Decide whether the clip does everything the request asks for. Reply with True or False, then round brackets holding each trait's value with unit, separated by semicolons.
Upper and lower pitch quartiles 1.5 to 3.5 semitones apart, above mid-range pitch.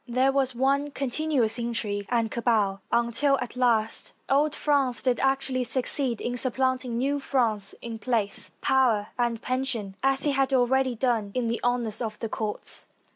True (2.7 semitones; 245 Hz)